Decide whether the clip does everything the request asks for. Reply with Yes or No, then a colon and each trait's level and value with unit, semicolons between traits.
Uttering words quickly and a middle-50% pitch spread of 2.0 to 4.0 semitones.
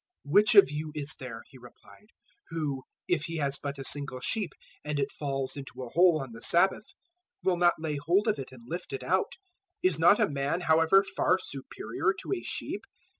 No: fast, 210 wpm; average, 4.6 semitones